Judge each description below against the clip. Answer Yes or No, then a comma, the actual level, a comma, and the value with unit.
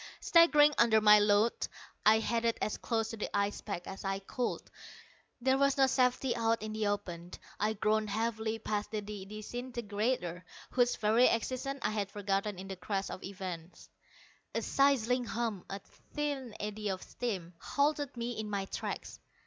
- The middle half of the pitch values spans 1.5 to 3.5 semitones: Yes, average, 3.2 semitones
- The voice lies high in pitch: Yes, high, 215 Hz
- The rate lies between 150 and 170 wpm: Yes, average, 165 wpm